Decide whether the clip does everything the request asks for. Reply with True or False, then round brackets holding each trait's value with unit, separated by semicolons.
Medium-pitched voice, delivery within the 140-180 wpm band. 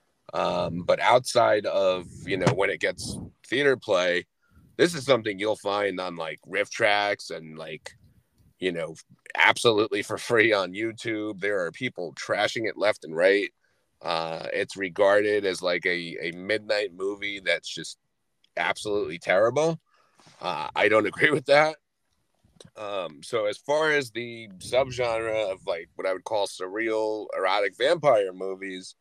False (105 Hz; 150 wpm)